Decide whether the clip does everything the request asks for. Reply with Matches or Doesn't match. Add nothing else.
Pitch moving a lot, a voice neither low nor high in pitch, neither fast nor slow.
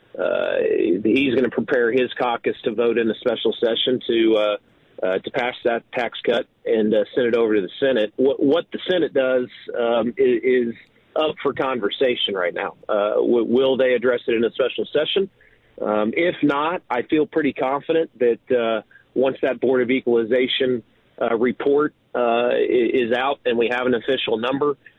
Doesn't match